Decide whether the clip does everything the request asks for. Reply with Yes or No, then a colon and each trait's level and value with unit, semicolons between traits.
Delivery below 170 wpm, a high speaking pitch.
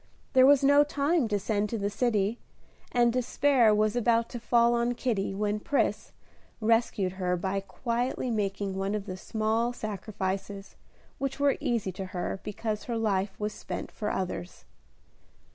Yes: average, 160 wpm; high, 215 Hz